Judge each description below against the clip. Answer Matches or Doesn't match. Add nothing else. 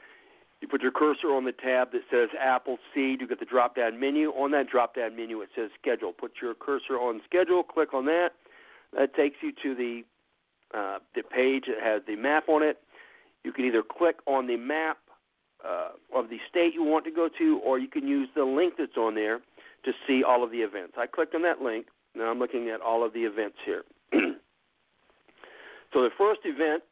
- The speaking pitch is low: Doesn't match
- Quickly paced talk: Matches